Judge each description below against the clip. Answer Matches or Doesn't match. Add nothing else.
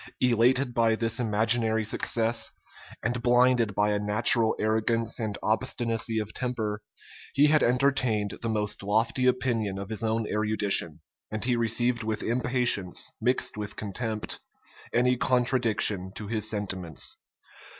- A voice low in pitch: Matches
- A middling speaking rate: Doesn't match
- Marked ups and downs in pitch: Doesn't match